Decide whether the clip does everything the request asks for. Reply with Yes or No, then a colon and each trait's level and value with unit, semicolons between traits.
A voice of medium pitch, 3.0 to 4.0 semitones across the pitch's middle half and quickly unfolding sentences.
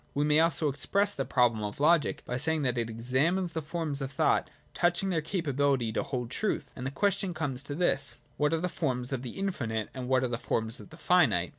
No: medium, 145 Hz; average, 4.9 semitones; fast, 235 wpm